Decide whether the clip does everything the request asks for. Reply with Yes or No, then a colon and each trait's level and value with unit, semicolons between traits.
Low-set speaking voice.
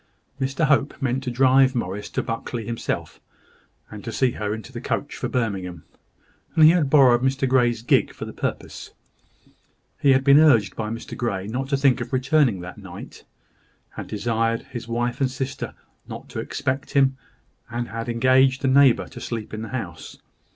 Yes: low, 125 Hz